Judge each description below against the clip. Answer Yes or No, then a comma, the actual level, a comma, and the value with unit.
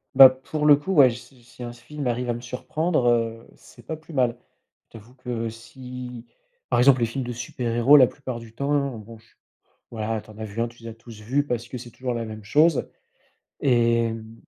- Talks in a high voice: No, low, 120 Hz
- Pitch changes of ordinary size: No, narrow, 2.3 semitones